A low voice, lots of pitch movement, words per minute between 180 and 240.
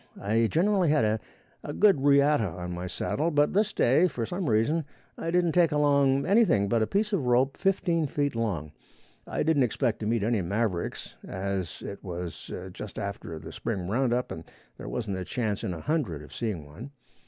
Yes: low, 120 Hz; wide, 7.3 semitones; average, 185 wpm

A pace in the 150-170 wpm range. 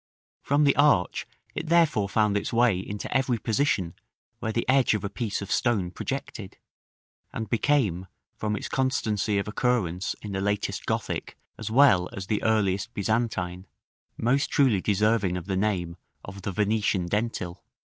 Yes: average, 155 wpm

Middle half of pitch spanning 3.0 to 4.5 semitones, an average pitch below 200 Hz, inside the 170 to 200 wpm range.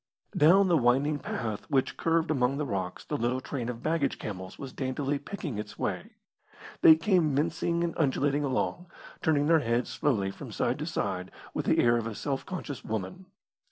No: average, 5.1 semitones; medium, 140 Hz; average, 185 wpm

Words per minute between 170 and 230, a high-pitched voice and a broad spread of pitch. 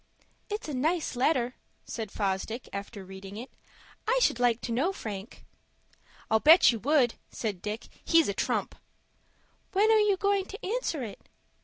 No: average, 160 wpm; high, 245 Hz; wide, 8.9 semitones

